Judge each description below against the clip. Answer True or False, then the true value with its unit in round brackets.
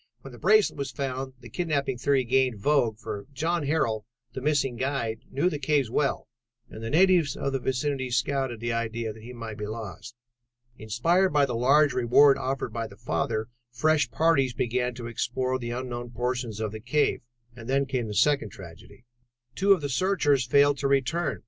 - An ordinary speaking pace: True (185 wpm)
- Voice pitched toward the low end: True (130 Hz)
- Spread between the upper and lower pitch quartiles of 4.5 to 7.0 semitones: False (3.5 semitones)